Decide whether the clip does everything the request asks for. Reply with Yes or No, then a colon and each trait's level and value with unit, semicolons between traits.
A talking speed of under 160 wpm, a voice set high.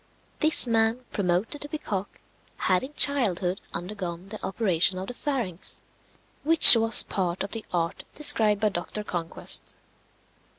Yes: average, 140 wpm; high, 205 Hz